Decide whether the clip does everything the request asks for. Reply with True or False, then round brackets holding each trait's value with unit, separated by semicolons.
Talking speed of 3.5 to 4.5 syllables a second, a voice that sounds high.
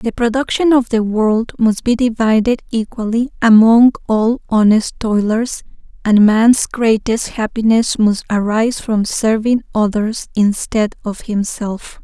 True (4.0 syllables/s; 225 Hz)